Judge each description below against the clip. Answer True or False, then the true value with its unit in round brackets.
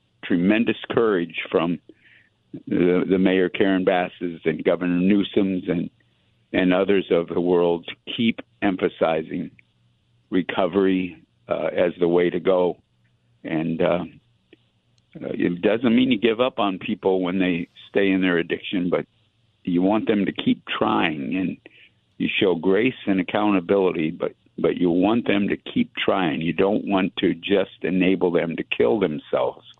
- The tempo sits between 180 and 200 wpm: False (150 wpm)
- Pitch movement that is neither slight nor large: False (2.0 semitones)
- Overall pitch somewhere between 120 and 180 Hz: False (95 Hz)